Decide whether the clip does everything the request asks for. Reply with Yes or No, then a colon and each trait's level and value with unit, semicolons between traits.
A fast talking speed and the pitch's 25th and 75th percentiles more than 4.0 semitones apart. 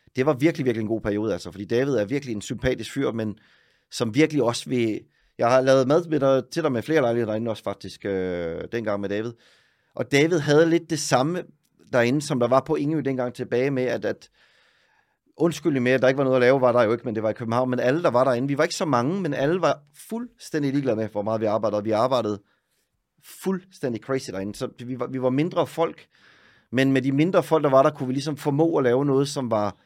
Yes: fast, 245 wpm; average, 4.7 semitones